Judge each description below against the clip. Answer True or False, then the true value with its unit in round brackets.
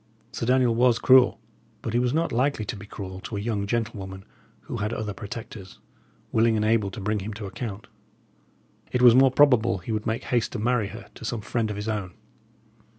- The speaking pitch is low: True (110 Hz)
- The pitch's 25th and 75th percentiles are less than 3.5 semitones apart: True (2.8 semitones)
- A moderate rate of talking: False (210 wpm)